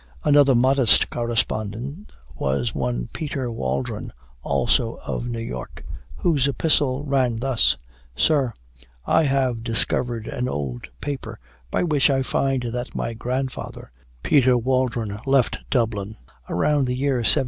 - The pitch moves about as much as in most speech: Yes, average, 3.1 semitones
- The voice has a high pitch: No, low, 125 Hz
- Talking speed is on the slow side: Yes, slow, 125 wpm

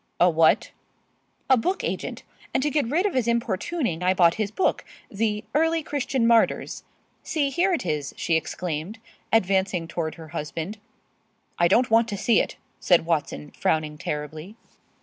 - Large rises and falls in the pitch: Yes, wide, 7.3 semitones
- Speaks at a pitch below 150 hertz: No, high, 195 Hz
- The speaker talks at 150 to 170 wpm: Yes, average, 160 wpm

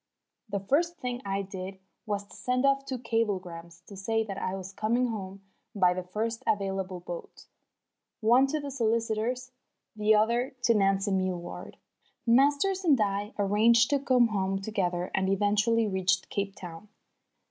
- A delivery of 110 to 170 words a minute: Yes, average, 155 wpm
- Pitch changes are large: No, average, 3.7 semitones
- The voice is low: No, high, 210 Hz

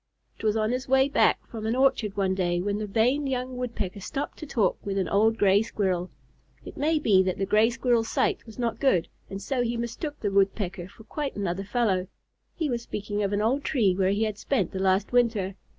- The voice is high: Yes, high, 215 Hz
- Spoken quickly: Yes, fast, 225 wpm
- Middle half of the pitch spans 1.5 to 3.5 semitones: No, average, 4.1 semitones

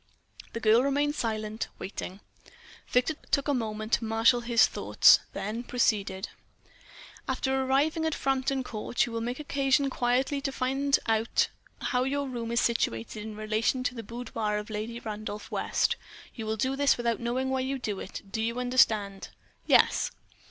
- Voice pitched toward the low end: No, high, 235 Hz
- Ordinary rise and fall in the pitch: Yes, average, 3.4 semitones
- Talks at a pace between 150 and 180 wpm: Yes, average, 160 wpm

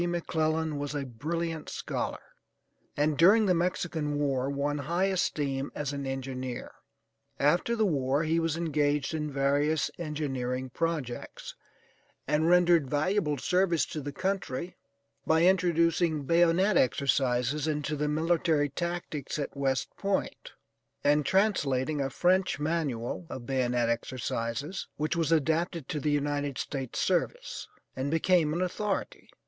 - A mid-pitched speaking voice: Yes, medium, 150 Hz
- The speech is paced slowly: Yes, slow, 130 wpm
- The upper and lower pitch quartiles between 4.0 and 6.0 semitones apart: No, average, 3.6 semitones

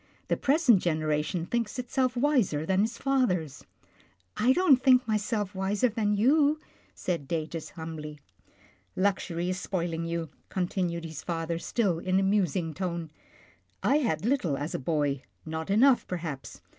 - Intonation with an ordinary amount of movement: No, wide, 6.3 semitones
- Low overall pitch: No, medium, 185 Hz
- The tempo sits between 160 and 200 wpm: No, average, 150 wpm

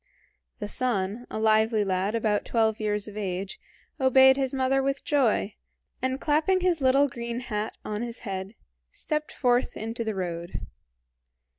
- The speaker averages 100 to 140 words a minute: No, average, 150 wpm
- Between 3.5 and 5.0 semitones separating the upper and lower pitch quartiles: Yes, average, 4.1 semitones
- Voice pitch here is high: Yes, high, 230 Hz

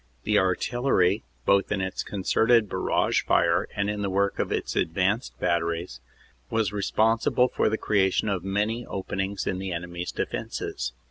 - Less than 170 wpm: Yes, average, 155 wpm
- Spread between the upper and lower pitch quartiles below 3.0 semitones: Yes, narrow, 2.5 semitones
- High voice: No, low, 100 Hz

